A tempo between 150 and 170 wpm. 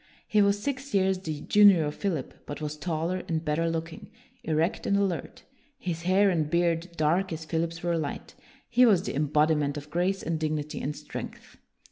No: average, 180 wpm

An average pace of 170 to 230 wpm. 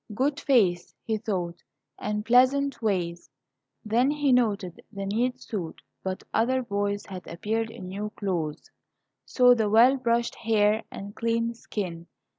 No: average, 140 wpm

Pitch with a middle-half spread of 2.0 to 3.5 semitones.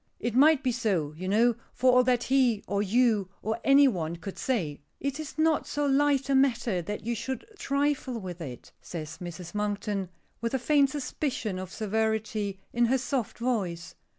No: wide, 5.4 semitones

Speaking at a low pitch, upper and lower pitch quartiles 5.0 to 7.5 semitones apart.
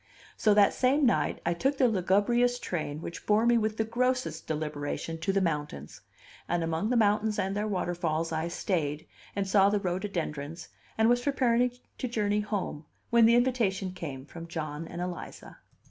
No: high, 195 Hz; wide, 5.6 semitones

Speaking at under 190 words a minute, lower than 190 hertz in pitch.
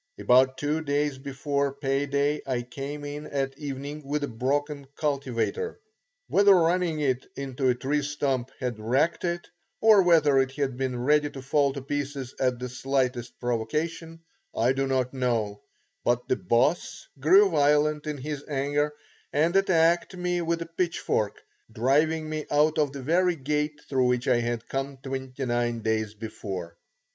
Yes: average, 160 wpm; medium, 140 Hz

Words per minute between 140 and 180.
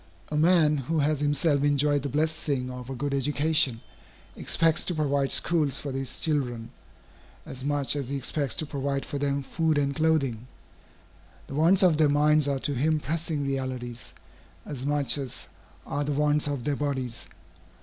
Yes: average, 170 wpm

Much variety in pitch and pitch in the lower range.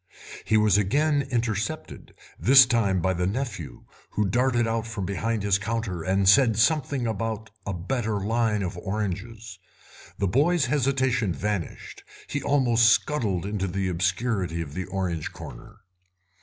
No: average, 4.0 semitones; low, 105 Hz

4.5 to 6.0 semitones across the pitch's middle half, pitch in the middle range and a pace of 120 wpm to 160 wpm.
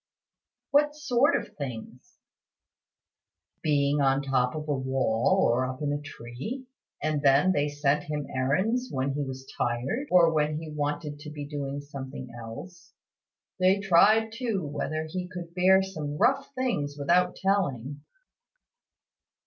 Yes: average, 5.2 semitones; medium, 150 Hz; average, 145 wpm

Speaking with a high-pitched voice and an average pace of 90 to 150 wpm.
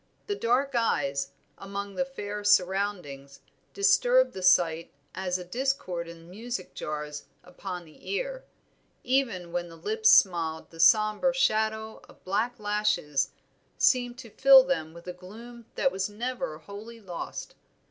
Yes: high, 205 Hz; average, 140 wpm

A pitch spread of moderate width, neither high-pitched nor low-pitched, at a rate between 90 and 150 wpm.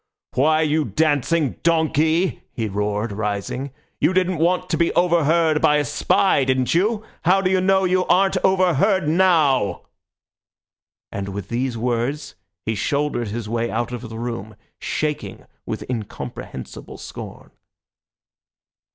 No: wide, 6.7 semitones; medium, 150 Hz; slow, 135 wpm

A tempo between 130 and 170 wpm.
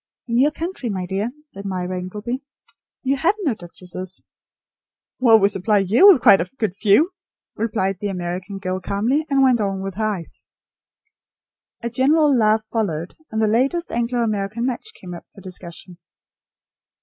Yes: average, 160 wpm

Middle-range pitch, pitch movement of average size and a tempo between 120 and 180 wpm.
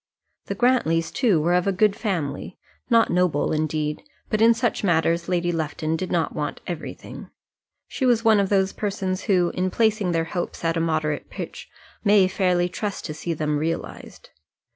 Yes: medium, 180 Hz; average, 3.8 semitones; average, 175 wpm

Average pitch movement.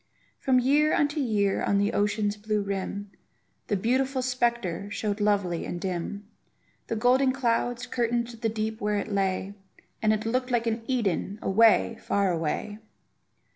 Yes: average, 3.2 semitones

